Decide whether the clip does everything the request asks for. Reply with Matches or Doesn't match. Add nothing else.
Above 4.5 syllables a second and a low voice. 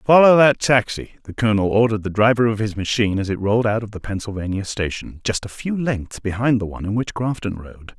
Matches